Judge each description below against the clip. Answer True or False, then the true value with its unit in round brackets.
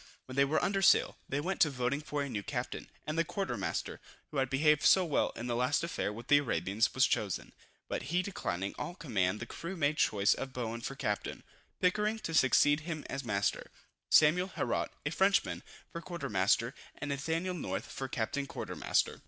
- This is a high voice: False (140 Hz)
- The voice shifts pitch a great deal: True (5.8 semitones)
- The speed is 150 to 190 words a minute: False (200 wpm)